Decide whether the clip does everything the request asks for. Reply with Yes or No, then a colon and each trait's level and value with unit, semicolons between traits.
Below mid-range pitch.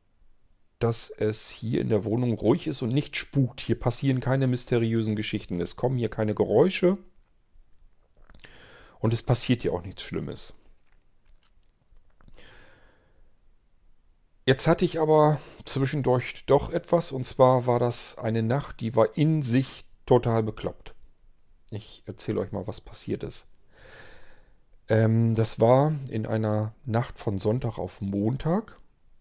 Yes: low, 120 Hz